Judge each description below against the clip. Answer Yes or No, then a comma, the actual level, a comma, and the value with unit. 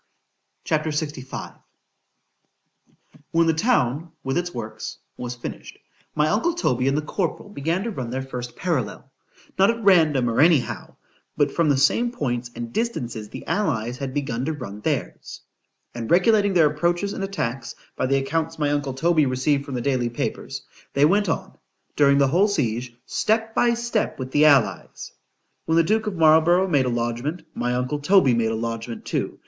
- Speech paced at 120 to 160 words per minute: No, average, 175 wpm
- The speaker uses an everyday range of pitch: No, wide, 5.8 semitones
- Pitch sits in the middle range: Yes, medium, 145 Hz